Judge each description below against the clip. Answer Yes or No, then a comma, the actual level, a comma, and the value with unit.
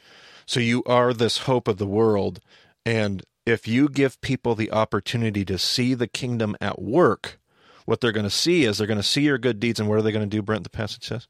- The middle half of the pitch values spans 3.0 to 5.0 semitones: No, narrow, 2.5 semitones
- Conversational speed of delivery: No, fast, 240 wpm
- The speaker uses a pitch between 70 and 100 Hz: No, low, 115 Hz